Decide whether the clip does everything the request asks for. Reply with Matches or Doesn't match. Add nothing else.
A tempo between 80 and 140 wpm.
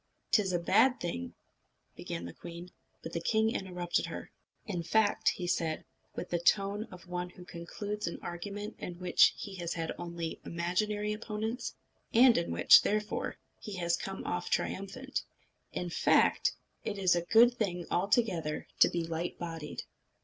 Doesn't match